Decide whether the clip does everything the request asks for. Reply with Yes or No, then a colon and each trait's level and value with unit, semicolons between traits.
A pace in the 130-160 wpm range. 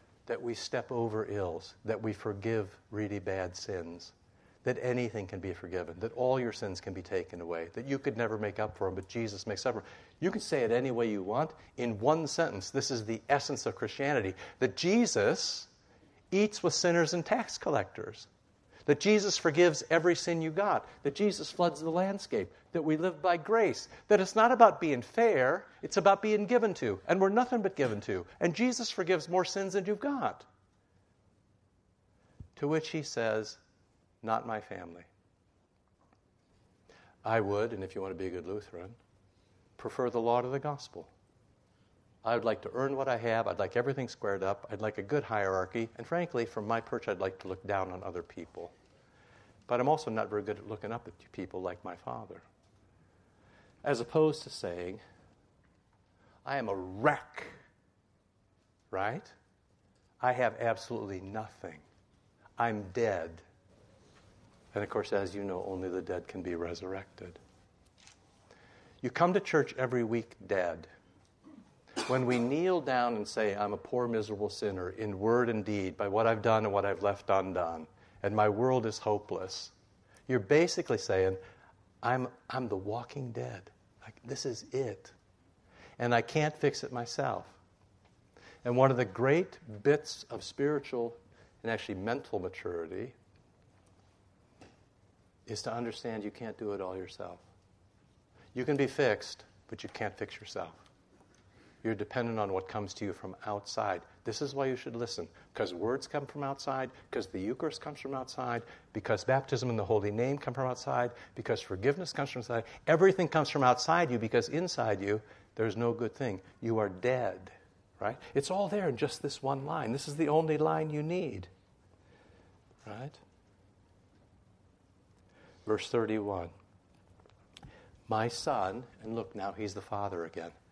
No: average, 170 wpm